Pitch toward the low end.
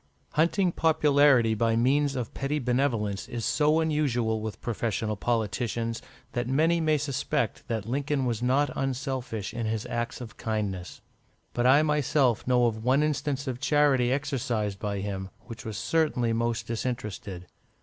Yes: low, 120 Hz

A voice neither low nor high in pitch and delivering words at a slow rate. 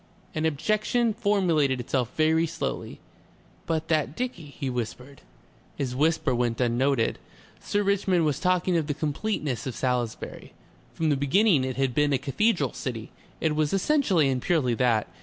No: medium, 150 Hz; average, 160 wpm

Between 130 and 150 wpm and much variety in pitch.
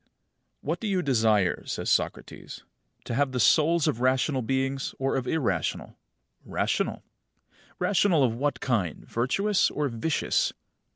No: slow, 135 wpm; average, 4.6 semitones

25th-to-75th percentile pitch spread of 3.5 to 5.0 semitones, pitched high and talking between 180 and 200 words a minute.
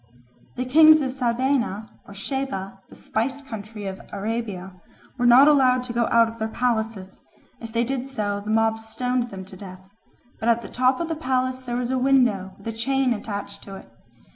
Yes: average, 4.0 semitones; high, 235 Hz; average, 195 wpm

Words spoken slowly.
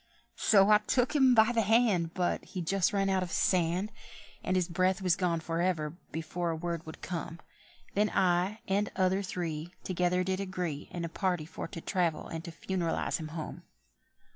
No: average, 185 wpm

